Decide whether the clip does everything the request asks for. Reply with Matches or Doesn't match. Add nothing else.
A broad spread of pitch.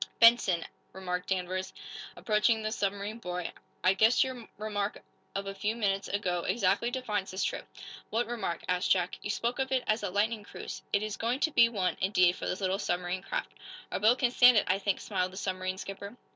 Doesn't match